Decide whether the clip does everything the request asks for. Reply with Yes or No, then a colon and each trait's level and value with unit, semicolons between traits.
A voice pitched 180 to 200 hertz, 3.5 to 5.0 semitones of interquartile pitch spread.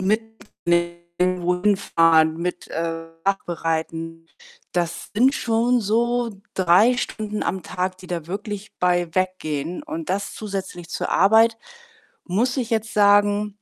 Yes: high, 190 Hz; average, 3.8 semitones